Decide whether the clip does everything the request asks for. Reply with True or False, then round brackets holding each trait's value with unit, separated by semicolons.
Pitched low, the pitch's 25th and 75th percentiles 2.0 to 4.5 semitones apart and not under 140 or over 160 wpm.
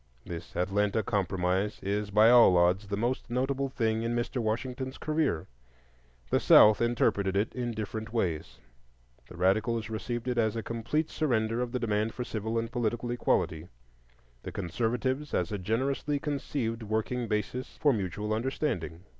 True (115 Hz; 3.3 semitones; 155 wpm)